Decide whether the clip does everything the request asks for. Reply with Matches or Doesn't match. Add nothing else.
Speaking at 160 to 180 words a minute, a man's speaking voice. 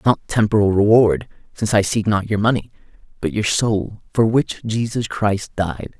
Matches